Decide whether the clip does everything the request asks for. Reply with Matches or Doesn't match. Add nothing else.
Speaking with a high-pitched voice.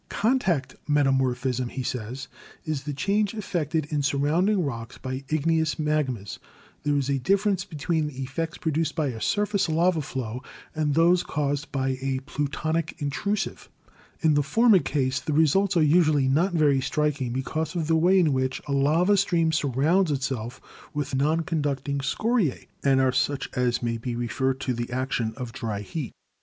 Doesn't match